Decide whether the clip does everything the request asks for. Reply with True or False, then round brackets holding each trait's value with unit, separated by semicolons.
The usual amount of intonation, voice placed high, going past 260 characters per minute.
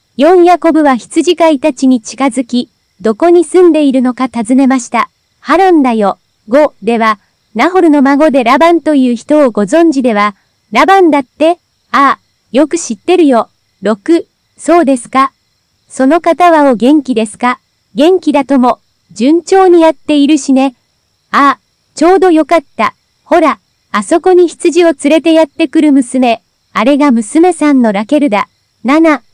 True (4.9 semitones; 290 Hz; 280 characters per minute)